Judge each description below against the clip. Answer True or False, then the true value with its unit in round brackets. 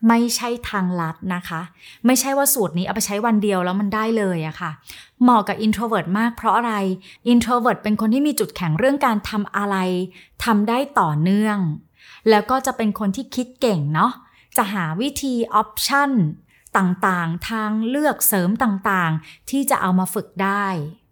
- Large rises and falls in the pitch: False (4.3 semitones)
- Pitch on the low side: False (210 Hz)